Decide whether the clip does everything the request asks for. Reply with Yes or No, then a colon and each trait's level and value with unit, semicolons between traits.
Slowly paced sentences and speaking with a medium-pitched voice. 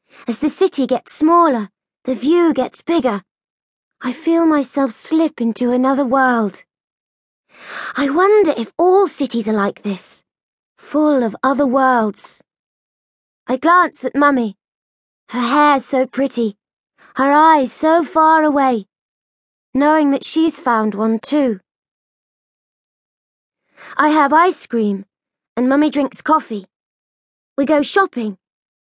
No: slow, 120 wpm; very high, 270 Hz